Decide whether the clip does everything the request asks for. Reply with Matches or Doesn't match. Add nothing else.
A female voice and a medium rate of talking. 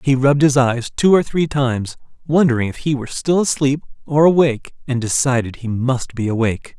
Doesn't match